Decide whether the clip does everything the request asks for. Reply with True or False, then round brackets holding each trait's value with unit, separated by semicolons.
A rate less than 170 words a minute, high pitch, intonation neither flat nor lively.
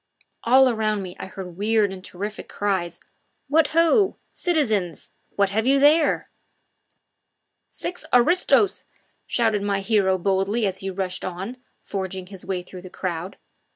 True (140 wpm; 200 Hz; 4.3 semitones)